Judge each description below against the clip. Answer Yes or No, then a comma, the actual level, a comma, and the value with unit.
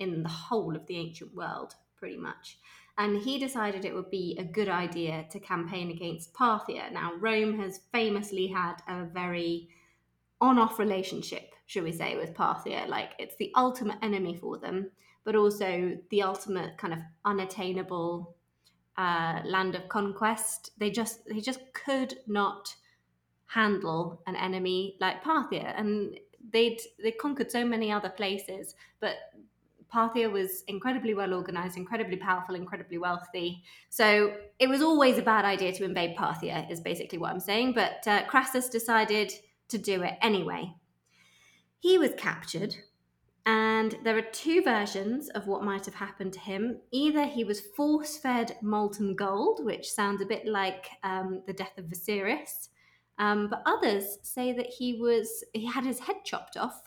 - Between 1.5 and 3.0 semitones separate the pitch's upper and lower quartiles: No, average, 3.5 semitones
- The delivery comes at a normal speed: Yes, average, 160 wpm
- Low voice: No, high, 205 Hz